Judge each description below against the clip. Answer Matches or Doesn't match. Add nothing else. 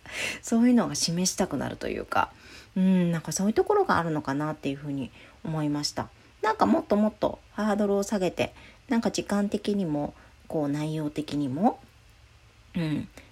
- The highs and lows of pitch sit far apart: Matches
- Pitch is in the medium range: Matches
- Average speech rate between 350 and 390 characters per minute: Matches